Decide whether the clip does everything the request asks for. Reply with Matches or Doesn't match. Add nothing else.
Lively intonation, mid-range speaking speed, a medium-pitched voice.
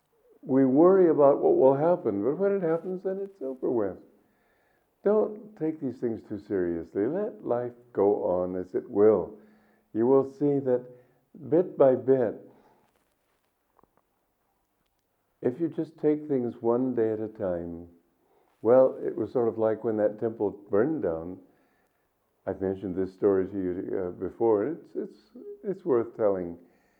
Doesn't match